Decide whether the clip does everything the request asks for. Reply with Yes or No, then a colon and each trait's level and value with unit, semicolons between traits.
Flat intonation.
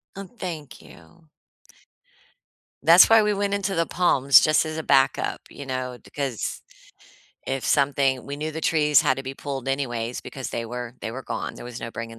No: average, 3.8 semitones